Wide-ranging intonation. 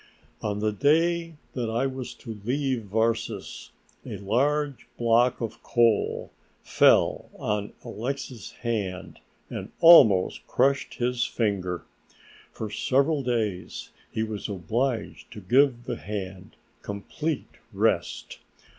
No: average, 4.3 semitones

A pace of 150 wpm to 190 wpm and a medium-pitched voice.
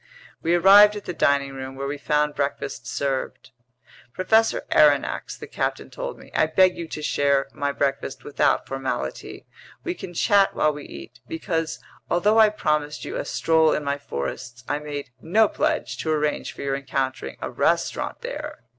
Yes: average, 175 wpm; medium, 150 Hz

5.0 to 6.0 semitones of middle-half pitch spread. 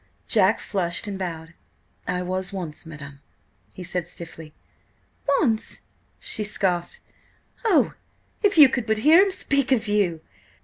Yes: wide, 5.4 semitones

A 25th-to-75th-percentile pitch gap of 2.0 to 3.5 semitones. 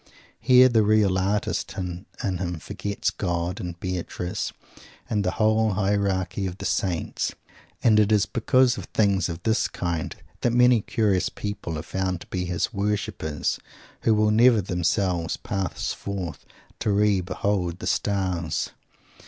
Yes: average, 3.0 semitones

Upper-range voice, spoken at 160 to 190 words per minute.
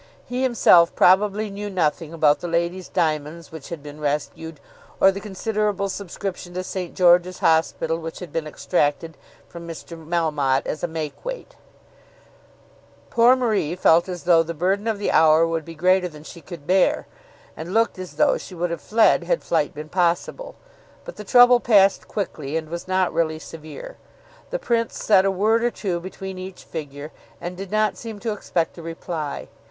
No: medium, 175 Hz; average, 180 wpm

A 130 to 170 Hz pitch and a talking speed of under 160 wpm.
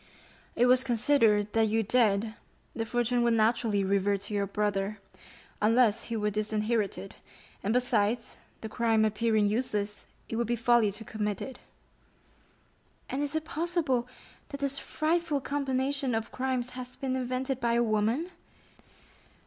No: high, 230 Hz; average, 145 wpm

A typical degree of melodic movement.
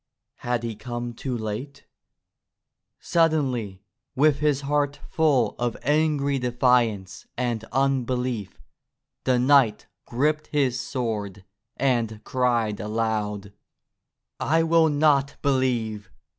Yes: average, 4.0 semitones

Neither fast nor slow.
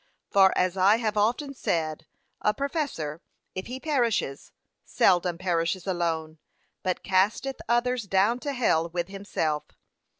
No: slow, 130 wpm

